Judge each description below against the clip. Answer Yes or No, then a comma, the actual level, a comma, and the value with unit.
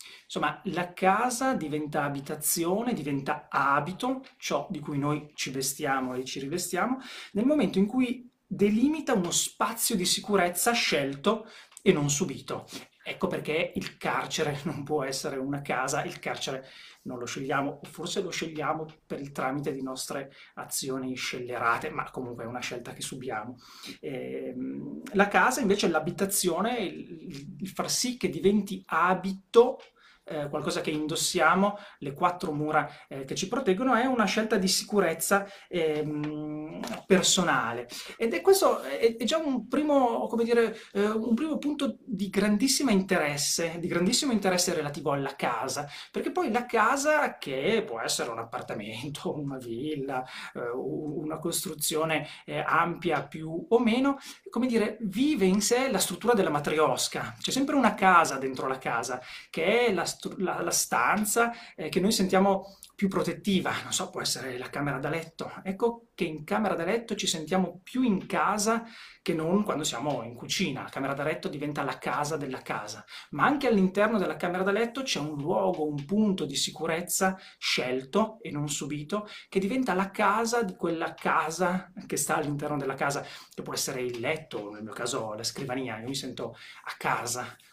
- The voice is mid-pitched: Yes, medium, 180 Hz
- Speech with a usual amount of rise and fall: No, wide, 6.0 semitones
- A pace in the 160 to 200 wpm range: Yes, average, 165 wpm